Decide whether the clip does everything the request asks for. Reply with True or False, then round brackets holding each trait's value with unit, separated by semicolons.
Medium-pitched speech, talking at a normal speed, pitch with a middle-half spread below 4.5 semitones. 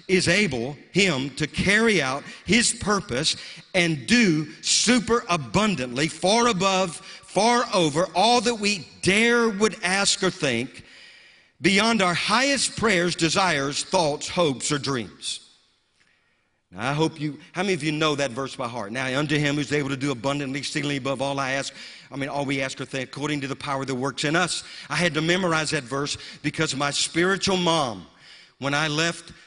False (160 Hz; 175 wpm; 5.3 semitones)